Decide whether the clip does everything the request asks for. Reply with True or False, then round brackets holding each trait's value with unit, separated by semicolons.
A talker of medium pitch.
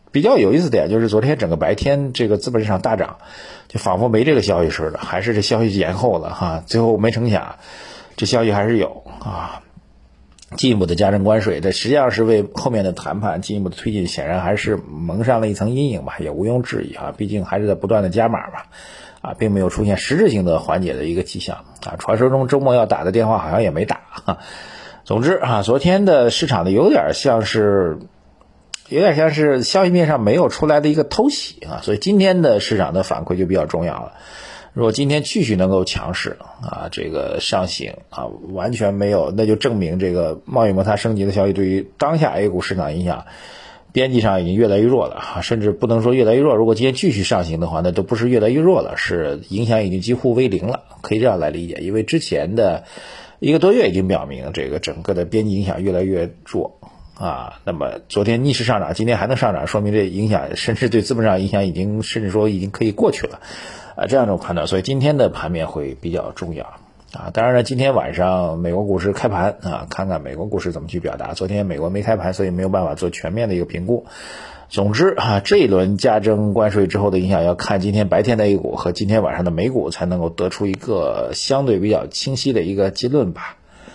False (105 Hz)